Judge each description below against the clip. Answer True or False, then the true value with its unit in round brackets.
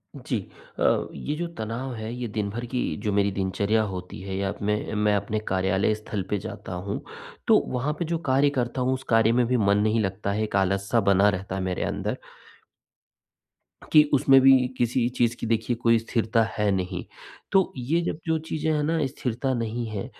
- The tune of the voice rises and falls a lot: False (4.0 semitones)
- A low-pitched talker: True (110 Hz)